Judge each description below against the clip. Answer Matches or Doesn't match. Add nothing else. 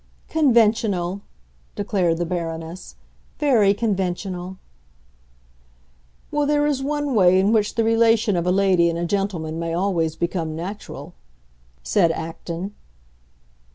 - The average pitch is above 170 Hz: Matches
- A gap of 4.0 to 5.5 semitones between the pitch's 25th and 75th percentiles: Matches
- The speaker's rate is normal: Doesn't match